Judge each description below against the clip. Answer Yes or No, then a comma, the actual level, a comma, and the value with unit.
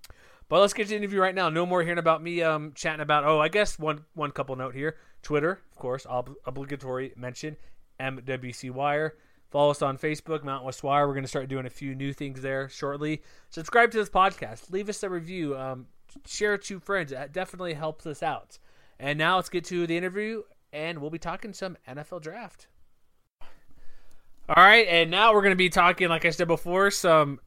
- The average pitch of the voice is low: No, medium, 155 Hz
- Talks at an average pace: No, fast, 210 wpm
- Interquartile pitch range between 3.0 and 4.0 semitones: No, average, 4.8 semitones